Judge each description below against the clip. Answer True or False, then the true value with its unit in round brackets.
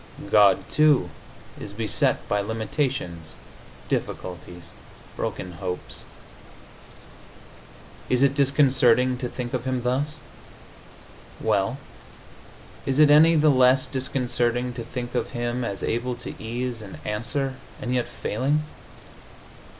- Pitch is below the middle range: True (125 Hz)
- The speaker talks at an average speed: False (110 wpm)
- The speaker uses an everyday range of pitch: True (3.4 semitones)